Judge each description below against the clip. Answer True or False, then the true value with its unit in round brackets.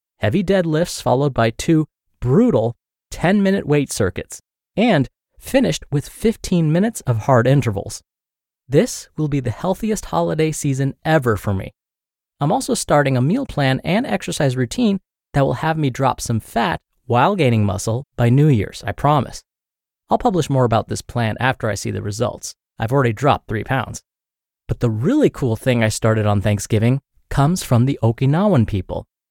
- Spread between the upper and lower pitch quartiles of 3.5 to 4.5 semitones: False (5.5 semitones)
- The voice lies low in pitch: True (130 Hz)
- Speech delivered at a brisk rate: False (170 wpm)